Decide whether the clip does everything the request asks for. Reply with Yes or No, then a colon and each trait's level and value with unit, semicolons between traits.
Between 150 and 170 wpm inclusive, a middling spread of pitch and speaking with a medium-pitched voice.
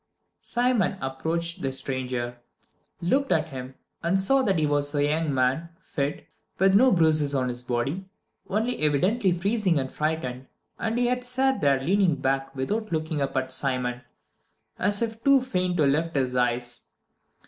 No: average, 160 wpm; wide, 6.7 semitones; medium, 155 Hz